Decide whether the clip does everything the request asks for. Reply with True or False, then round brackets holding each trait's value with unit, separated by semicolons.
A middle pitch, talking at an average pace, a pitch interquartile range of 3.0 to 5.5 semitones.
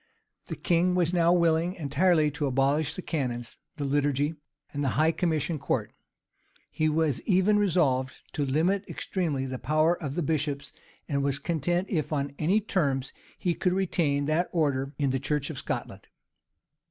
True (155 Hz; 165 wpm; 3.7 semitones)